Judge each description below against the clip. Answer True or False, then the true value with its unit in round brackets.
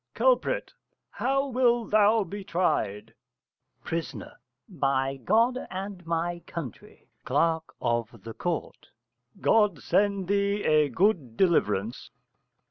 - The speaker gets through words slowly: True (105 wpm)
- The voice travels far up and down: True (7.0 semitones)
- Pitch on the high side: False (180 Hz)